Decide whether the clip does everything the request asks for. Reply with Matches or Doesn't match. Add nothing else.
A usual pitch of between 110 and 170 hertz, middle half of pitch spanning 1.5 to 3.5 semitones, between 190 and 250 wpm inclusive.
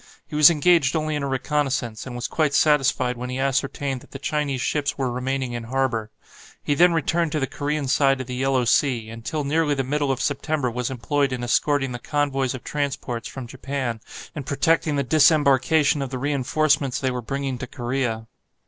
Matches